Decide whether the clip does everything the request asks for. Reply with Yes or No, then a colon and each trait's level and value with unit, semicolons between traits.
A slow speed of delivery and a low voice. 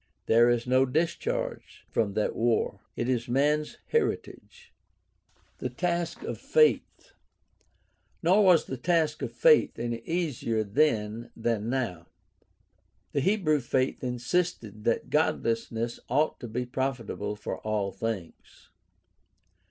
Yes: slow, 120 wpm; low, 125 Hz